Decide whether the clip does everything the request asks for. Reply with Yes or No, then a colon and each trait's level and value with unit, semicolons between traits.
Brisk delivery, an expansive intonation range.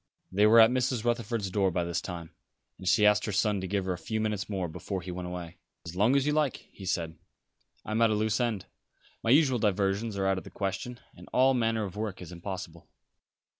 No: fast, 235 wpm; average, 3.5 semitones